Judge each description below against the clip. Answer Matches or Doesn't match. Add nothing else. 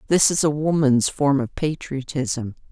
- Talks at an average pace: Matches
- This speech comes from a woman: Matches